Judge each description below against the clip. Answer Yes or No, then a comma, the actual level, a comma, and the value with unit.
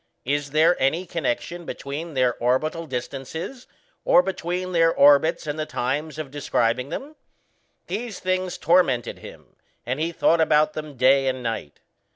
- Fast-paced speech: No, average, 150 wpm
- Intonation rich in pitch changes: No, average, 4.2 semitones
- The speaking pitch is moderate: Yes, medium, 155 Hz